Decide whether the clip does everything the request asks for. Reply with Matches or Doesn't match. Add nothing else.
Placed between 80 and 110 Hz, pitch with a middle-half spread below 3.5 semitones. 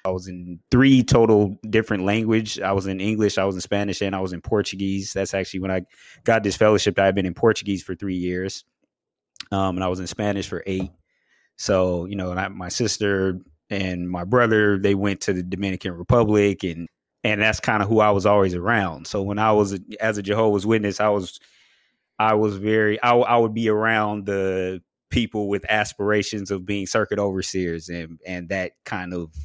Matches